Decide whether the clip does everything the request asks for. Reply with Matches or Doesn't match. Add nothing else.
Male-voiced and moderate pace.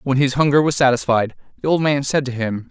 Doesn't match